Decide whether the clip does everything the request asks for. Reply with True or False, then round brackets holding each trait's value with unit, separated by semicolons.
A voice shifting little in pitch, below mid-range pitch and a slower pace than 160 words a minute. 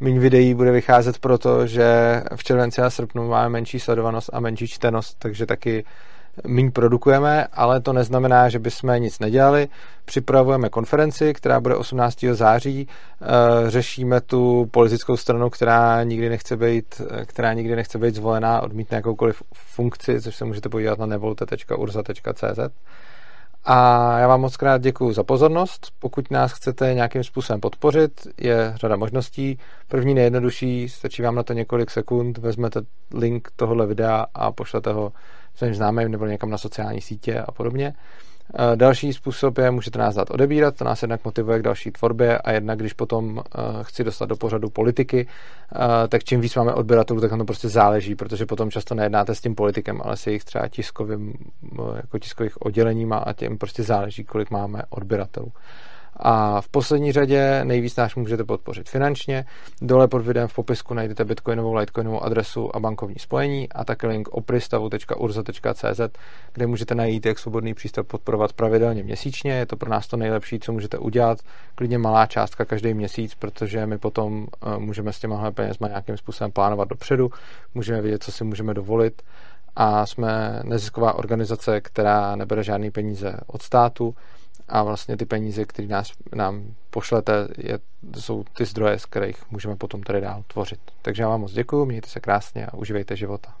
False (2.2 semitones; 115 Hz; 165 wpm)